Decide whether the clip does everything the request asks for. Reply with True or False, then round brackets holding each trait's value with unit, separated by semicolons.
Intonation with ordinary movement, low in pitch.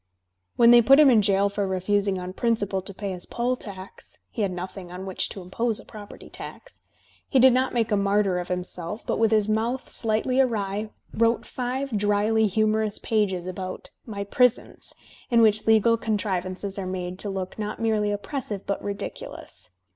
False (3.0 semitones; 210 Hz)